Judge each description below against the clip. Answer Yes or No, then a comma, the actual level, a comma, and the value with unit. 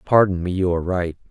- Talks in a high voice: No, very low, 90 Hz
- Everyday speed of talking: No, fast, 230 wpm